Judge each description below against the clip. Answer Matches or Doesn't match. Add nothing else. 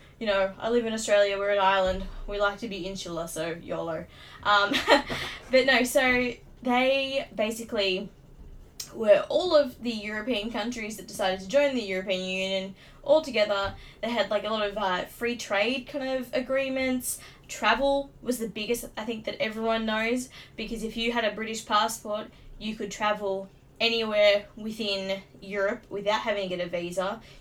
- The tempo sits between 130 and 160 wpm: Doesn't match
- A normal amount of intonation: Matches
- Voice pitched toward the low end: Doesn't match